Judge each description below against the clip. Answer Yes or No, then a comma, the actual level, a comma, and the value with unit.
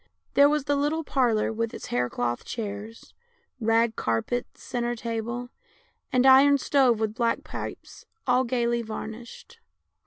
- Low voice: No, high, 235 Hz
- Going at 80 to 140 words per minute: Yes, slow, 135 wpm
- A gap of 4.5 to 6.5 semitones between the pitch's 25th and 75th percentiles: No, average, 2.9 semitones